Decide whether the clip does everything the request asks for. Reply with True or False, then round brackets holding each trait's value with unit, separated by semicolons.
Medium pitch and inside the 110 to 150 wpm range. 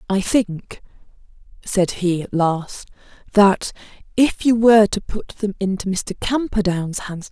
False (200 Hz; 140 wpm)